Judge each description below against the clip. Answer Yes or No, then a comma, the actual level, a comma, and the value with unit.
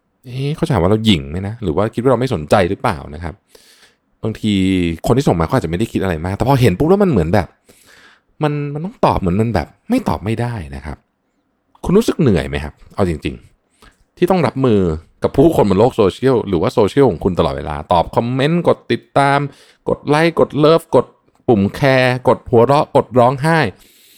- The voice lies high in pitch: No, low, 115 Hz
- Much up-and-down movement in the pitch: Yes, wide, 6.9 semitones